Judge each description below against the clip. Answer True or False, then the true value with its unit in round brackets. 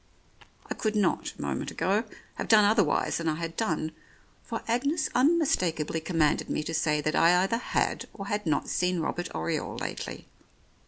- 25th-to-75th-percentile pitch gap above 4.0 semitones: True (5.3 semitones)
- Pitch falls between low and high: True (180 Hz)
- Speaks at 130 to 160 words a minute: False (170 wpm)